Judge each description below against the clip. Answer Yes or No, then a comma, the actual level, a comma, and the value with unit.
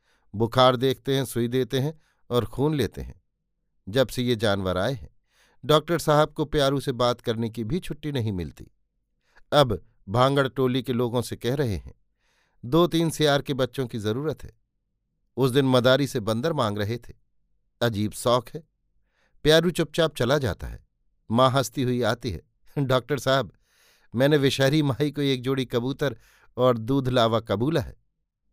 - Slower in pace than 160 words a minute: No, average, 170 wpm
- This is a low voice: Yes, low, 130 Hz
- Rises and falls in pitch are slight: No, average, 3.8 semitones